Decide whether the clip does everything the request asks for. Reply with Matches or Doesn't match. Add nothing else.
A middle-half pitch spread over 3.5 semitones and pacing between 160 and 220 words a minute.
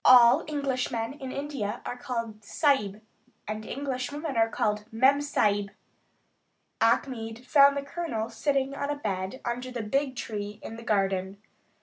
Doesn't match